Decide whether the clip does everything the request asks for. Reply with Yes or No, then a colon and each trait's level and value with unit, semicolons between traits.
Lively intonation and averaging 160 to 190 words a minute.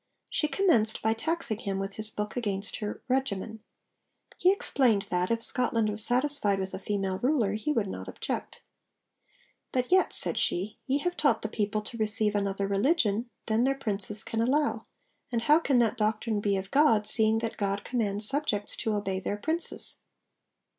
No: average, 3.9 semitones; average, 175 wpm